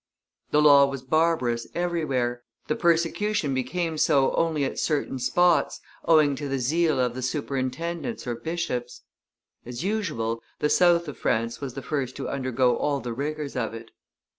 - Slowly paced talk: No, average, 160 wpm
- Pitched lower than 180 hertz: Yes, medium, 140 Hz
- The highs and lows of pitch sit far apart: No, average, 4.6 semitones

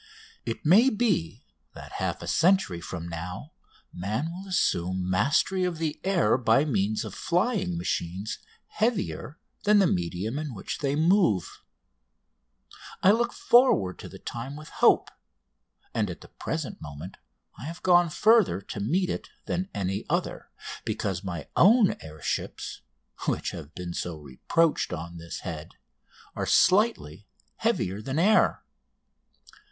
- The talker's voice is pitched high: No, low, 125 Hz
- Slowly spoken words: No, average, 145 wpm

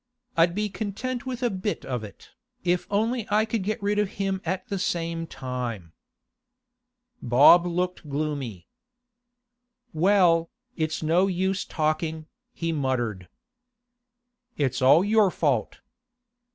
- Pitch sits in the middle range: Yes, medium, 180 Hz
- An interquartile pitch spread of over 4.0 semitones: Yes, average, 5.3 semitones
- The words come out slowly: Yes, slow, 125 wpm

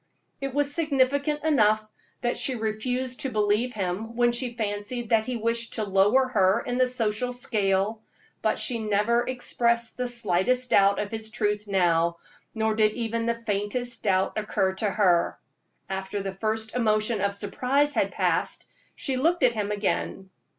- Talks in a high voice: Yes, high, 220 Hz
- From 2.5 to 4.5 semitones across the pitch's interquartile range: Yes, average, 3.3 semitones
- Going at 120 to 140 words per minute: No, average, 165 wpm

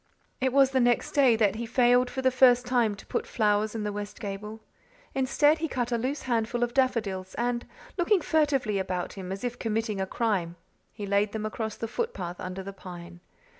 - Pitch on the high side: Yes, high, 225 Hz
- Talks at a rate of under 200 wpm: No, fast, 205 wpm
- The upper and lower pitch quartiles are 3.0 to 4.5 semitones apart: Yes, average, 4.0 semitones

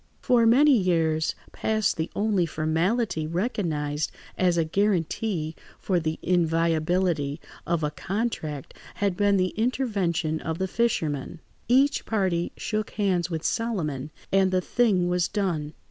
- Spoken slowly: Yes, slow, 130 wpm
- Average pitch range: Yes, average, 4.7 semitones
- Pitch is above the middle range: No, medium, 180 Hz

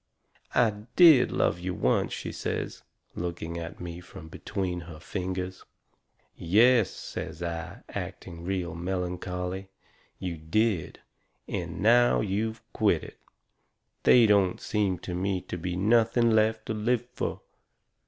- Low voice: Yes, very low, 95 Hz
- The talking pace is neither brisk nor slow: No, slow, 130 wpm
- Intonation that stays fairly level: No, average, 3.8 semitones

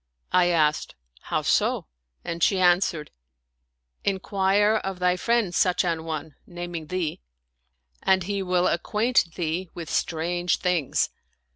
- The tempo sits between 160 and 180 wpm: No, average, 145 wpm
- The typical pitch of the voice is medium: Yes, medium, 175 Hz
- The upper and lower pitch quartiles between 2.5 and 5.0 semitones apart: Yes, average, 2.8 semitones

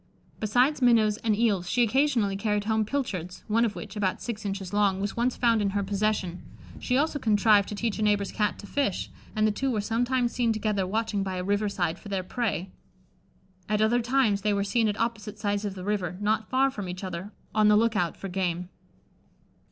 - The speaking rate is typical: No, fast, 215 wpm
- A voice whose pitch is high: Yes, high, 210 Hz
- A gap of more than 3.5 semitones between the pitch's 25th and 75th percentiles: No, narrow, 2.6 semitones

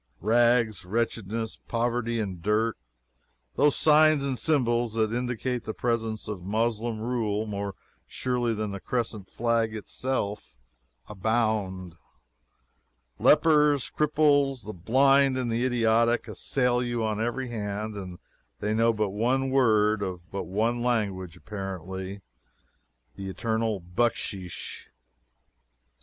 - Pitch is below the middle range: Yes, low, 115 Hz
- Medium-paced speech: No, slow, 115 wpm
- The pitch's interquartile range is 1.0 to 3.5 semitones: Yes, average, 3.0 semitones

